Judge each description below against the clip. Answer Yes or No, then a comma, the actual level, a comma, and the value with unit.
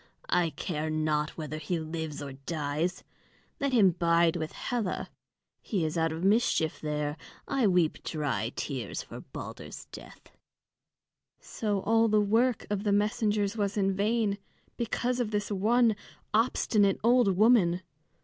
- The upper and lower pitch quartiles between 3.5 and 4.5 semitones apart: No, wide, 5.5 semitones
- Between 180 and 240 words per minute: No, average, 140 wpm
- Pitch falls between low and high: No, high, 195 Hz